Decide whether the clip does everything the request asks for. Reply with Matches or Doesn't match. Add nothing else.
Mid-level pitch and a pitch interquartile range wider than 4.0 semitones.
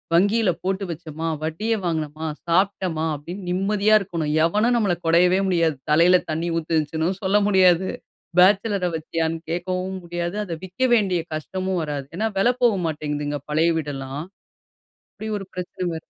Doesn't match